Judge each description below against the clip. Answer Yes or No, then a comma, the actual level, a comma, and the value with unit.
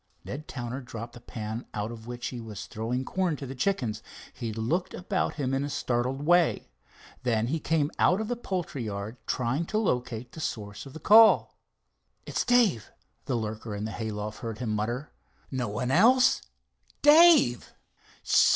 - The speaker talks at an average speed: Yes, average, 170 wpm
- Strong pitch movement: Yes, wide, 6.3 semitones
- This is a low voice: Yes, low, 125 Hz